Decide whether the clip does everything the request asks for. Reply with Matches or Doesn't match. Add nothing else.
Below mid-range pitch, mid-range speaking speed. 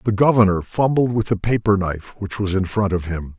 Doesn't match